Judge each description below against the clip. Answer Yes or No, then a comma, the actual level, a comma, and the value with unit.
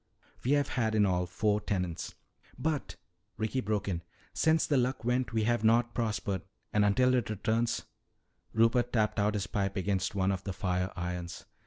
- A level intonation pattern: No, average, 3.6 semitones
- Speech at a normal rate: Yes, average, 180 wpm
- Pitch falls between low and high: No, low, 105 Hz